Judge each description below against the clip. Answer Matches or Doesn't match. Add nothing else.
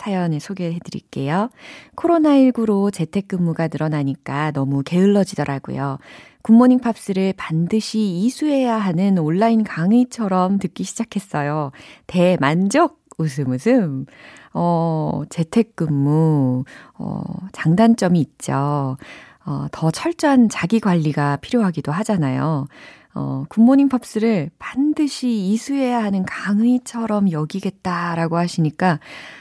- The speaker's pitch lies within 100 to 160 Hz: Doesn't match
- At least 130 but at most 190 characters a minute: Doesn't match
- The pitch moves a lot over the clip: Matches